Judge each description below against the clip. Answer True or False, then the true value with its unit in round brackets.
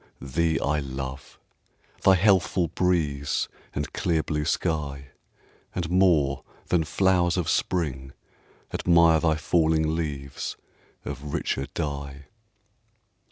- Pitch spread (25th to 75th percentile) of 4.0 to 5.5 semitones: False (3.5 semitones)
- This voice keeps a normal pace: False (105 wpm)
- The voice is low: True (80 Hz)